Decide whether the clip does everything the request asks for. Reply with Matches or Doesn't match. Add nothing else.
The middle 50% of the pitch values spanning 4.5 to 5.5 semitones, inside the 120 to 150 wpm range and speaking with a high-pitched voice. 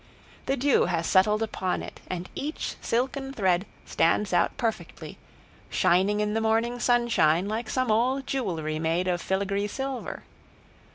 Matches